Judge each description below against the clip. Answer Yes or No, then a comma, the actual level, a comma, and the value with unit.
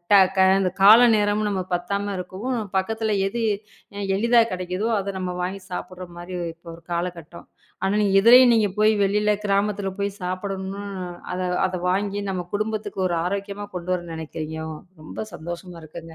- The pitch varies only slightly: Yes, narrow, 2.3 semitones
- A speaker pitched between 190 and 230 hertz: Yes, high, 195 Hz